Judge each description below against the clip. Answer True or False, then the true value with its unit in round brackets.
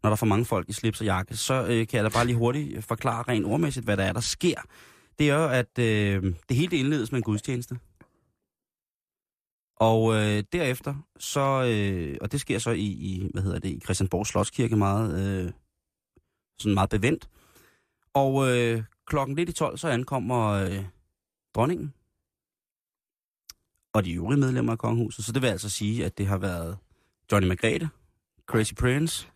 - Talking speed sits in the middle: True (180 wpm)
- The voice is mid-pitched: False (110 Hz)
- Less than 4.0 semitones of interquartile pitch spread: False (4.3 semitones)